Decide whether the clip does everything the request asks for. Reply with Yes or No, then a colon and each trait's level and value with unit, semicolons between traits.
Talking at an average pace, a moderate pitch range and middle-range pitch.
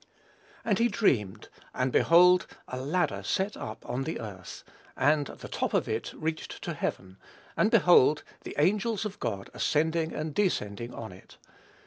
No: average, 155 wpm; wide, 7.6 semitones; medium, 155 Hz